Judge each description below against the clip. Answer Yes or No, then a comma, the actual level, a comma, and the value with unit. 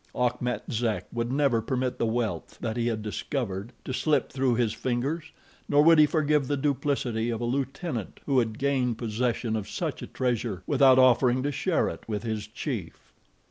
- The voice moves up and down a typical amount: Yes, average, 3.3 semitones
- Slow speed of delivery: No, average, 180 wpm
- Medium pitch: No, low, 125 Hz